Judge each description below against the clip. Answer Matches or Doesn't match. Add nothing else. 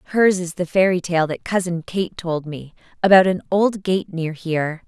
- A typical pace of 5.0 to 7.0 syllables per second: Doesn't match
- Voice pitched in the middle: Matches